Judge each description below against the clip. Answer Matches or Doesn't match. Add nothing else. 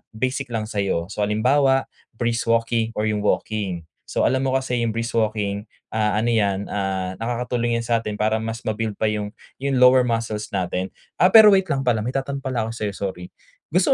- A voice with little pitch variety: Doesn't match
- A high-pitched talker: Doesn't match